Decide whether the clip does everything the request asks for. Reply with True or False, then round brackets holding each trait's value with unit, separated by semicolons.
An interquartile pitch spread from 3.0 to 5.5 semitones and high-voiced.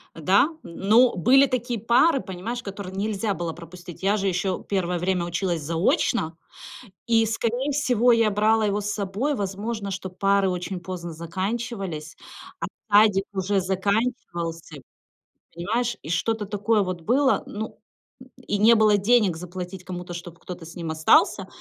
True (4.0 semitones; 195 Hz)